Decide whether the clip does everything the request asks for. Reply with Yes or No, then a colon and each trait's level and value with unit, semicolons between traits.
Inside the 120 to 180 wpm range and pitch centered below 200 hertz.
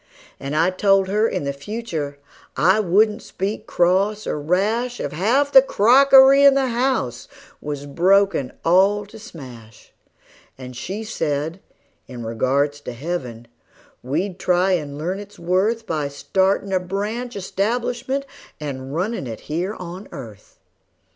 Yes: average, 140 wpm; medium, 185 Hz